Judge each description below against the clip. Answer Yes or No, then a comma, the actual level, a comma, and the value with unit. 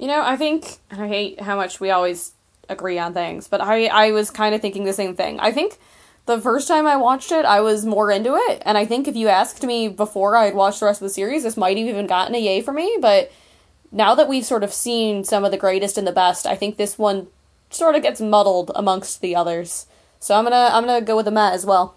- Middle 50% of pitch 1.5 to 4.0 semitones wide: Yes, average, 3.4 semitones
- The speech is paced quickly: Yes, fast, 260 wpm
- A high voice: Yes, high, 210 Hz